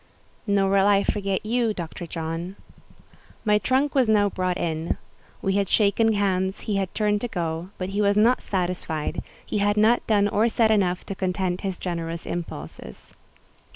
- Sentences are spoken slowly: No, average, 170 wpm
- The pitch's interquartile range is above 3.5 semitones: No, average, 2.9 semitones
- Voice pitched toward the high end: Yes, high, 195 Hz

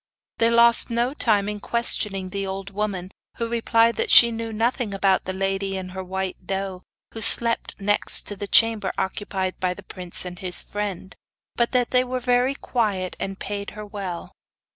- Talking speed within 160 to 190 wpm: Yes, average, 180 wpm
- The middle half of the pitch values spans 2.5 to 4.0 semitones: Yes, average, 3.3 semitones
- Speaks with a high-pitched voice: Yes, high, 205 Hz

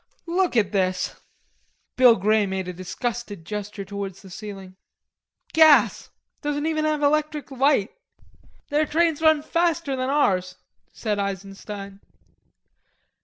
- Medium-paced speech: No, slow, 120 wpm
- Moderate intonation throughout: No, wide, 7.4 semitones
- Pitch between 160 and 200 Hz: No, high, 225 Hz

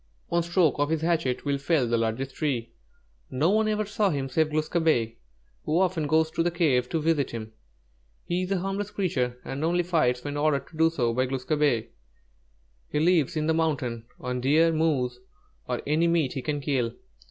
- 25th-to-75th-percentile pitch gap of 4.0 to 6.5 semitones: Yes, average, 4.5 semitones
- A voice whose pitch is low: No, medium, 150 Hz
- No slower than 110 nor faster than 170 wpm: No, average, 200 wpm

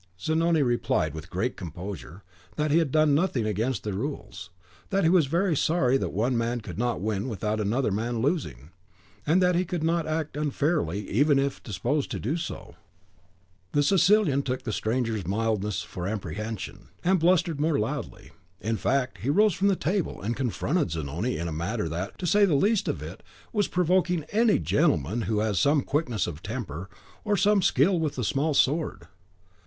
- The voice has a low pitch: Yes, low, 130 Hz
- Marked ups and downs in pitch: Yes, wide, 7.7 semitones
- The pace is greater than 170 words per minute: Yes, average, 185 wpm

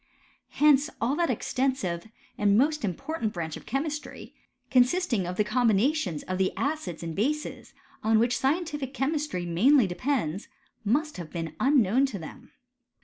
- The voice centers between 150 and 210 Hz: No, high, 245 Hz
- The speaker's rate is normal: Yes, average, 145 wpm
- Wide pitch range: Yes, wide, 7.5 semitones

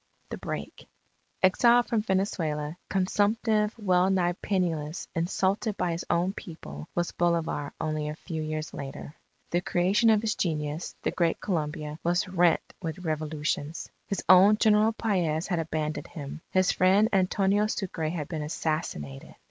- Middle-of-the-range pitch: Yes, medium, 175 Hz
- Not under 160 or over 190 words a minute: No, average, 140 wpm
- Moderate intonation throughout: Yes, average, 3.9 semitones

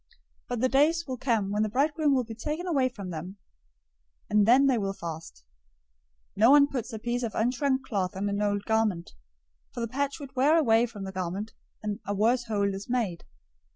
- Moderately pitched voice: No, high, 225 Hz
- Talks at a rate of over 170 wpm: Yes, fast, 205 wpm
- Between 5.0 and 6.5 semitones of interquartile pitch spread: No, average, 4.6 semitones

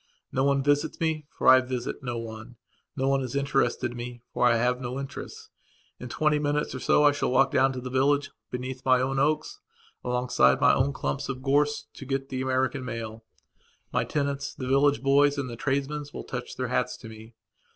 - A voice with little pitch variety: Yes, narrow, 2.2 semitones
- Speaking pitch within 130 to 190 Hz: Yes, low, 135 Hz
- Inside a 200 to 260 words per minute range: Yes, fast, 205 wpm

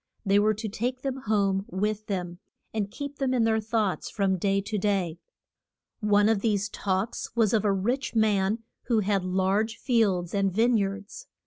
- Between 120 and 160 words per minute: No, average, 180 wpm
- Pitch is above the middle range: Yes, high, 210 Hz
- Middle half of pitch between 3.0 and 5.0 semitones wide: No, narrow, 2.5 semitones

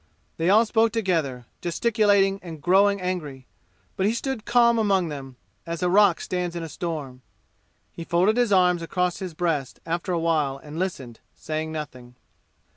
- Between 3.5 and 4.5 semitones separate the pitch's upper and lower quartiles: Yes, average, 4.1 semitones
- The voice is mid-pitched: Yes, medium, 175 Hz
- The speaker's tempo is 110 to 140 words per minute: No, average, 165 wpm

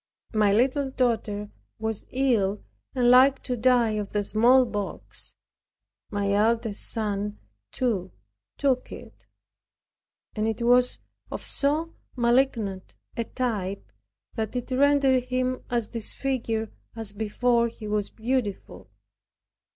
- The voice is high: Yes, high, 230 Hz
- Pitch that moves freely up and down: No, average, 3.4 semitones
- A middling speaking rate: No, slow, 110 wpm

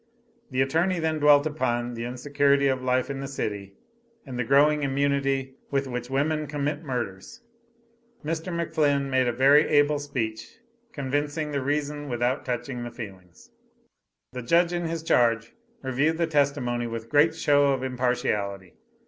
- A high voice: No, medium, 140 Hz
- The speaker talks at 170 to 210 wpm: No, average, 150 wpm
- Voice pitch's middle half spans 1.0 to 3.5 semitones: Yes, average, 3.2 semitones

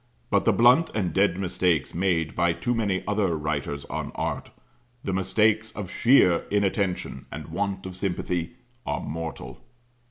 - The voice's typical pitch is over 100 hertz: No, very low, 95 Hz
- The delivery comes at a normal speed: Yes, average, 150 wpm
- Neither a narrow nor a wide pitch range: Yes, average, 3.3 semitones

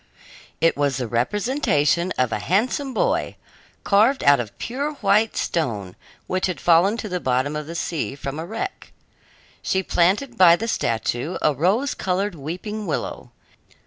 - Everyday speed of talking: Yes, average, 155 wpm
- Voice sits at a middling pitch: Yes, medium, 180 Hz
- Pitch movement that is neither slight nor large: No, wide, 7.0 semitones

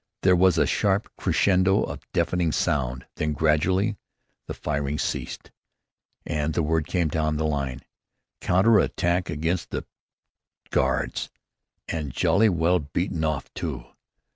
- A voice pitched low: Yes, very low, 80 Hz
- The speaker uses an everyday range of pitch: Yes, average, 3.5 semitones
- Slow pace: Yes, slow, 125 wpm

